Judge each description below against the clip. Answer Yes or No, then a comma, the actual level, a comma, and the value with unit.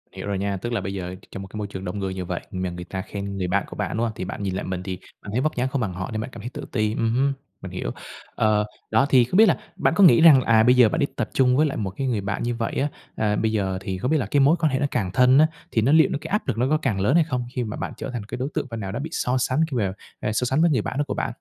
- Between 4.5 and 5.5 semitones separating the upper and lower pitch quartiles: Yes, average, 5.1 semitones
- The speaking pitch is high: No, low, 115 Hz